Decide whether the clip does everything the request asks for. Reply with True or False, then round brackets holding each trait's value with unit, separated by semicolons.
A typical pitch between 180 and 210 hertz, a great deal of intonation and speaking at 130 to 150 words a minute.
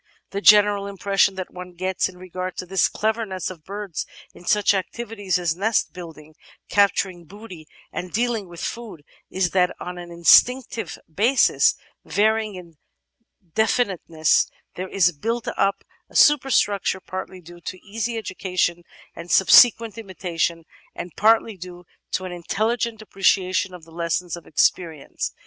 False (185 Hz; 3.2 semitones; 145 wpm)